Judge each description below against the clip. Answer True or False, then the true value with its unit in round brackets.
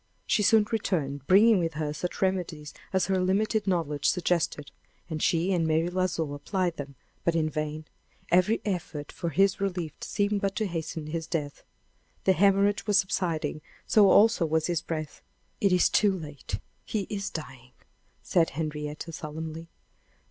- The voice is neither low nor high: True (170 Hz)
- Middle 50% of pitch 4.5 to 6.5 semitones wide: False (4.0 semitones)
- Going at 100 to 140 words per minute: False (155 wpm)